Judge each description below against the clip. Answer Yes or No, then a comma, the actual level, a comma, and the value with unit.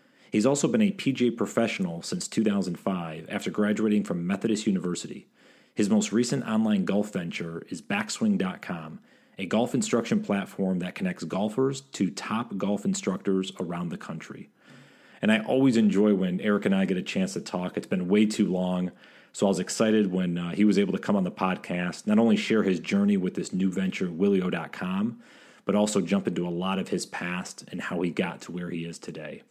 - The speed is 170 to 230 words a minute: Yes, average, 195 wpm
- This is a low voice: Yes, low, 105 Hz